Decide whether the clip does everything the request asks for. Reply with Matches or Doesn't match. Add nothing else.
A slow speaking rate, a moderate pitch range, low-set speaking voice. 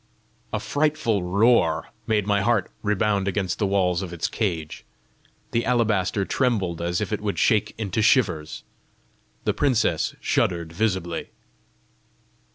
Matches